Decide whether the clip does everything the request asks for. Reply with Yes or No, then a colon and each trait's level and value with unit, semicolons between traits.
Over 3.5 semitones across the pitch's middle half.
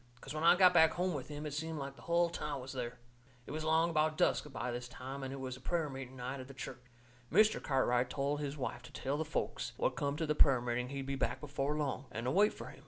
No: average, 3.1 semitones